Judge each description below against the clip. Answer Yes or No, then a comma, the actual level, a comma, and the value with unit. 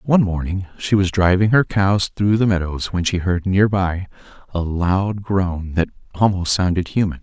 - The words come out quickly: No, average, 185 wpm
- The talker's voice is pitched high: No, very low, 95 Hz